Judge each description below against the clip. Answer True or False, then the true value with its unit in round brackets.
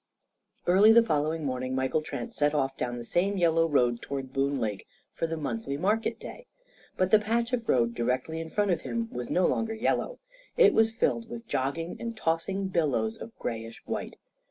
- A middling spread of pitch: False (8.8 semitones)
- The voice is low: False (165 Hz)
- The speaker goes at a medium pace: True (190 wpm)